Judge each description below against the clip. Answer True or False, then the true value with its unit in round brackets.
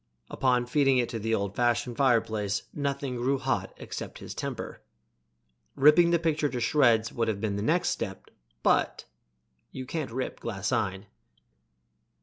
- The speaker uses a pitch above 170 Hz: False (120 Hz)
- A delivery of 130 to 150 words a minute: True (145 wpm)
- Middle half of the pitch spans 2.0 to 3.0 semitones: False (3.9 semitones)